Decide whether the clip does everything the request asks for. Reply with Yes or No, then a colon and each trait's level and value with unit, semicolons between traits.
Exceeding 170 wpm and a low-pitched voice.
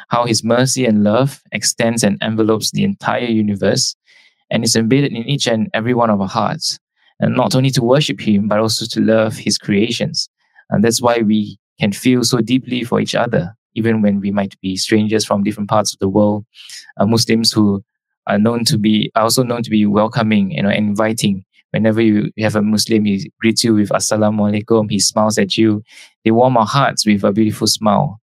Yes: fast, 205 wpm; low, 110 Hz